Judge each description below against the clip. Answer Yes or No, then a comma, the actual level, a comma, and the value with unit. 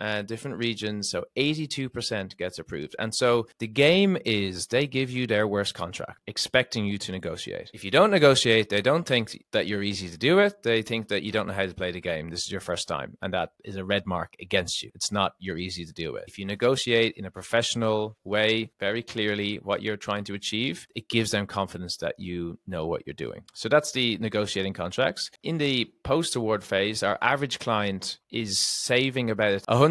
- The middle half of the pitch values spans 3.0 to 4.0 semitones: Yes, average, 3.5 semitones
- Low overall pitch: Yes, low, 110 Hz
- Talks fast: Yes, fast, 215 wpm